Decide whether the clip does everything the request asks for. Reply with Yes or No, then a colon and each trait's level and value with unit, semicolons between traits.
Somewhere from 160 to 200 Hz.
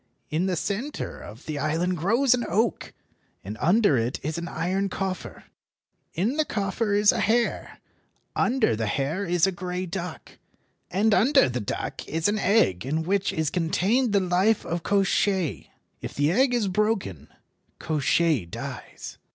Yes: medium, 185 Hz